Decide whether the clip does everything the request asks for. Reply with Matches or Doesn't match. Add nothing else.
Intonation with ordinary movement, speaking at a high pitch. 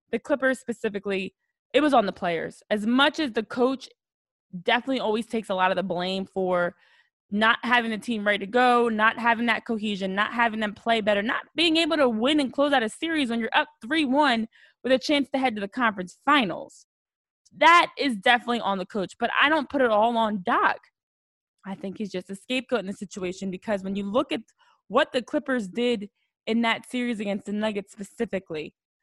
Matches